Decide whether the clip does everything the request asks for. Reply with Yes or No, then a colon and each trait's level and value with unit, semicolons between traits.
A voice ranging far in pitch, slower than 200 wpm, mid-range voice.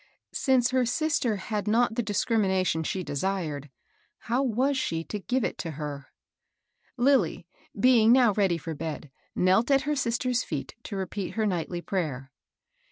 No: wide, 6.4 semitones; average, 165 wpm; high, 205 Hz